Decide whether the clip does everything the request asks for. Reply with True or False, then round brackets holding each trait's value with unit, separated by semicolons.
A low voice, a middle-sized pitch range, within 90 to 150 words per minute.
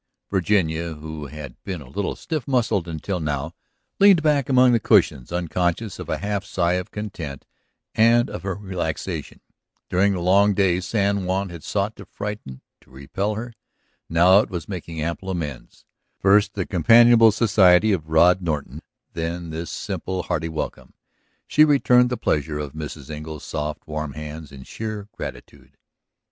False (90 Hz; 4.9 semitones; 160 wpm)